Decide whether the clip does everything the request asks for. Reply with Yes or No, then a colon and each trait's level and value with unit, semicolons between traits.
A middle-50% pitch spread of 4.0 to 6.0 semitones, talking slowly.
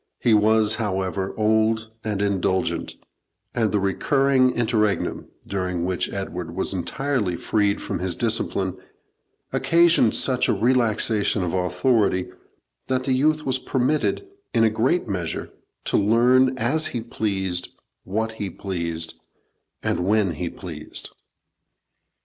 Yes: average, 4.7 semitones; slow, 125 wpm